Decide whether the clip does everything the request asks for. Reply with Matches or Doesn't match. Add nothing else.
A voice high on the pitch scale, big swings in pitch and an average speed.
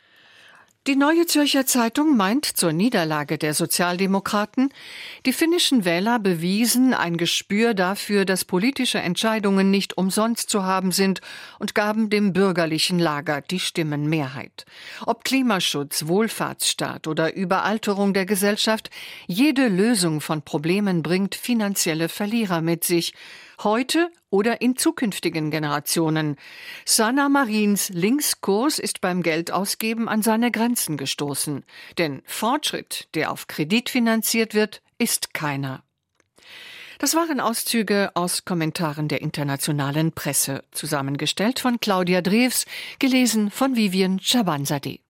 Doesn't match